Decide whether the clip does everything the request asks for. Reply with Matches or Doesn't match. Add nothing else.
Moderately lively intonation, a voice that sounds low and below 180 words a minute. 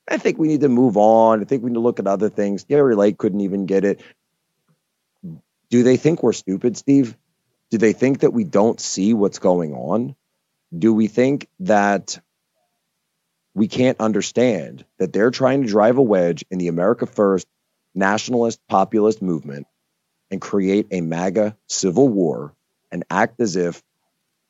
Matches